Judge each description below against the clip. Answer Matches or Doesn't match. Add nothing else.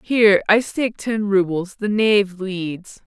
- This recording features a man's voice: Doesn't match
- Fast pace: Doesn't match